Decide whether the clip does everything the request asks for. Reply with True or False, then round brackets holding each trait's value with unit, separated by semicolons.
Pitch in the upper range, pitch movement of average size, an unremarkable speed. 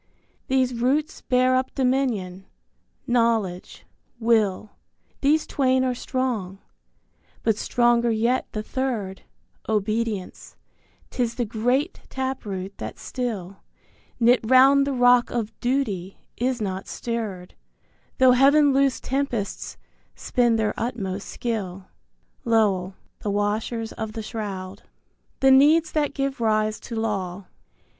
False (235 Hz; 3.9 semitones; 120 wpm)